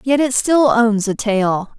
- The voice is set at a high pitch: Yes, high, 230 Hz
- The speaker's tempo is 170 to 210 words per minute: Yes, average, 200 wpm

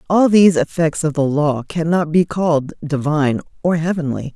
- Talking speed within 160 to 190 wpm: Yes, average, 165 wpm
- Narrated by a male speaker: No, female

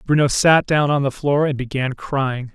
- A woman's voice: No, male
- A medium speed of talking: No, fast, 210 wpm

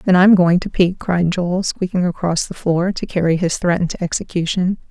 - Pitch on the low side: No, medium, 180 Hz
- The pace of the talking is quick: Yes, fast, 210 wpm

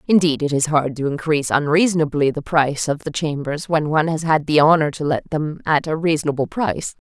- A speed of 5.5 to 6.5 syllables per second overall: Yes, 5.9 syllables/s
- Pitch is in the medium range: Yes, medium, 150 Hz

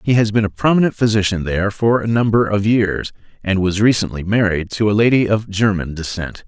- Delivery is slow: No, fast, 205 wpm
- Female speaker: No, male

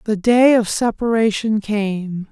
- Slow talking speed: Yes, slow, 130 wpm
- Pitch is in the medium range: No, high, 215 Hz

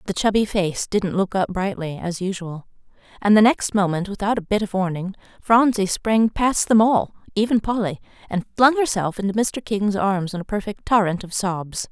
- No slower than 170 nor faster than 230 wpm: Yes, average, 195 wpm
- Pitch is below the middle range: No, high, 200 Hz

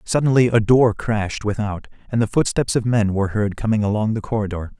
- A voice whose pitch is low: Yes, low, 110 Hz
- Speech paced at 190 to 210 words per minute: Yes, average, 200 wpm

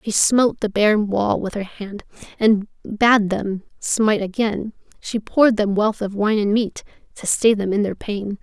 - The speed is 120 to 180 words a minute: No, average, 190 wpm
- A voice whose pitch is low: No, high, 210 Hz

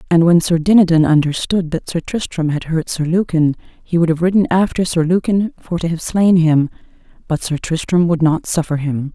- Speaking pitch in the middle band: Yes, medium, 170 Hz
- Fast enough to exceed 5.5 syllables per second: No, 5.2 syllables/s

